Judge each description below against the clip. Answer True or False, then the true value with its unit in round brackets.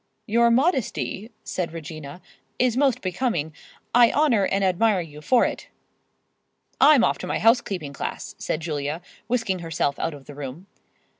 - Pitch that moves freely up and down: True (7.2 semitones)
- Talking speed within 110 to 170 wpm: True (150 wpm)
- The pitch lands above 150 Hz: True (190 Hz)